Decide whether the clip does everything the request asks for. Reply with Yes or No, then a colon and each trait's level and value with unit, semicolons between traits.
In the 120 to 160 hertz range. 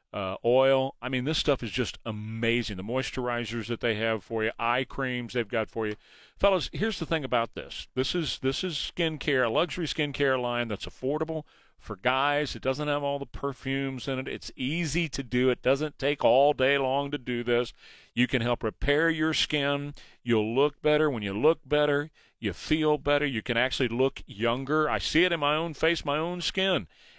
Yes: low, 135 Hz